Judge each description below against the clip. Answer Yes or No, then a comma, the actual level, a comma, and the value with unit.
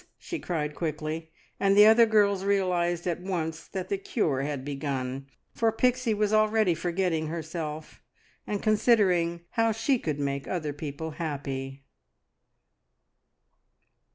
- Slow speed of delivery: Yes, slow, 125 wpm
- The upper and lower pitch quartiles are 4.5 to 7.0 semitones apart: Yes, wide, 5.4 semitones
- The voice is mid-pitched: Yes, medium, 170 Hz